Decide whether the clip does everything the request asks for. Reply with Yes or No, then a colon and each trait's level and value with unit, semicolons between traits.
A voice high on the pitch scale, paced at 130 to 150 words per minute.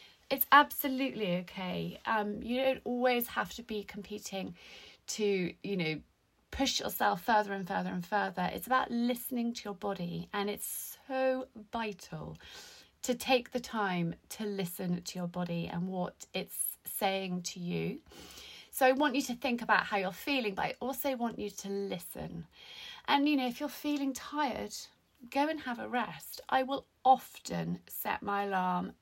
No: high, 210 Hz; average, 180 wpm